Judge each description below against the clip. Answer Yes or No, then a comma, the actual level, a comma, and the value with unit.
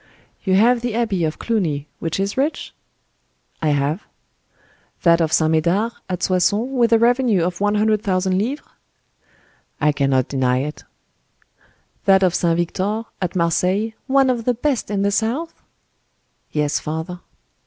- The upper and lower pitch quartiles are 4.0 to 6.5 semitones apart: Yes, wide, 5.6 semitones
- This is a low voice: No, high, 190 Hz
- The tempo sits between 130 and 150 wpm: Yes, average, 145 wpm